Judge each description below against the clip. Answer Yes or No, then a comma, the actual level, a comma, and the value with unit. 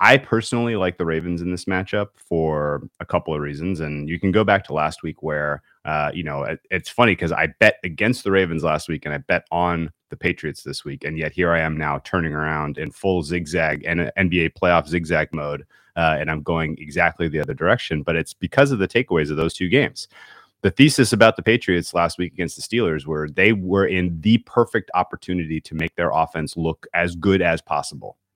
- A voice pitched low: Yes, very low, 85 Hz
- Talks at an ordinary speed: No, fast, 220 wpm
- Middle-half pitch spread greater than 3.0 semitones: Yes, average, 3.5 semitones